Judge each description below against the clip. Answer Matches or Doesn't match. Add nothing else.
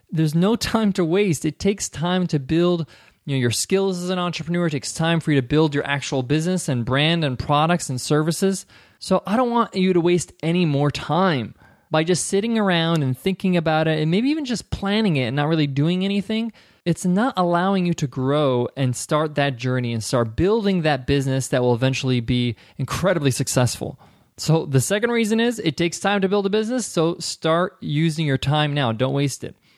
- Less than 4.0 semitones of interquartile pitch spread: Doesn't match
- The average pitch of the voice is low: Doesn't match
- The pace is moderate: Doesn't match